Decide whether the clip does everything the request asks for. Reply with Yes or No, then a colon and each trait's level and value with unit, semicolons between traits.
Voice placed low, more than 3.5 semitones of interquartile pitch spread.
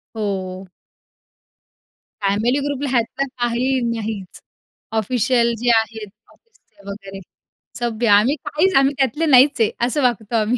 No: high, 235 Hz; average, 4.0 semitones